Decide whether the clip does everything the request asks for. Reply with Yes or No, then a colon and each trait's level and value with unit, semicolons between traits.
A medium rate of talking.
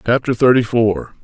Yes: average, 145 wpm